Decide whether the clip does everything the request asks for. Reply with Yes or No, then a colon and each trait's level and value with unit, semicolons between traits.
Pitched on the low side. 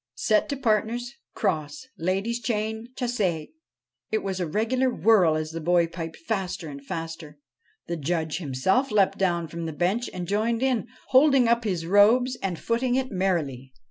No: high, 195 Hz